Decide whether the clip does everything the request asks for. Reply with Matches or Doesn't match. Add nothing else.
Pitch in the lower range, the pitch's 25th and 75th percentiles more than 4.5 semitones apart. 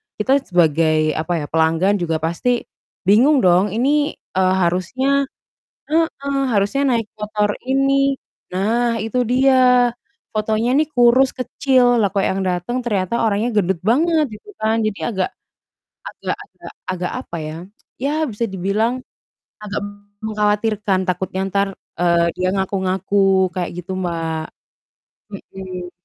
Doesn't match